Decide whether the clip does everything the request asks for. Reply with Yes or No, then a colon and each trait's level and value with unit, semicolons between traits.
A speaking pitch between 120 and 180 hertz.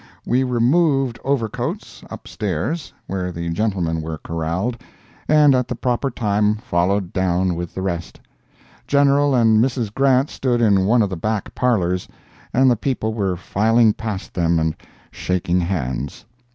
No: low, 105 Hz